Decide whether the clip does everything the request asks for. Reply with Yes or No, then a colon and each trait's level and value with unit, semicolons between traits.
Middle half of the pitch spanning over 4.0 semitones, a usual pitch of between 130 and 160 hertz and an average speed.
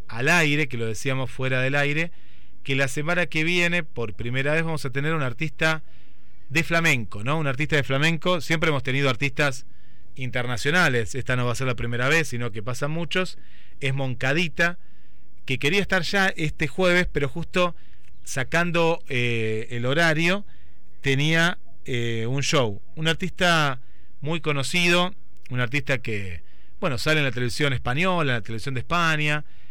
Yes: average, 5.3 semitones; medium, 140 Hz; average, 165 wpm